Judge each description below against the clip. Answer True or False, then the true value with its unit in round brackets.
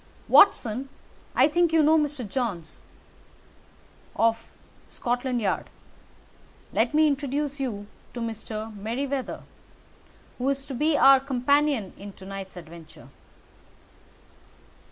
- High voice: True (255 Hz)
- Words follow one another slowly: True (110 wpm)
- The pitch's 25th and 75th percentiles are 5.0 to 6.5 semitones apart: False (4.6 semitones)